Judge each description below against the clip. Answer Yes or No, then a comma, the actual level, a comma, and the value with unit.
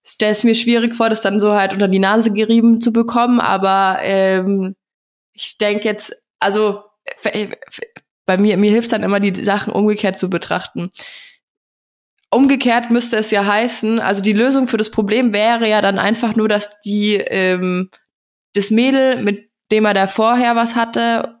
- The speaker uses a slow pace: No, average, 175 wpm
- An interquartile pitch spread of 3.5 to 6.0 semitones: No, narrow, 2.4 semitones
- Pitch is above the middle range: Yes, high, 215 Hz